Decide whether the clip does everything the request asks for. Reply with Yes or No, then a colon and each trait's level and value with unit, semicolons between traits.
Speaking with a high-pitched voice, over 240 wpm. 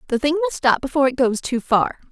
Yes: very high, 255 Hz; fast, 255 wpm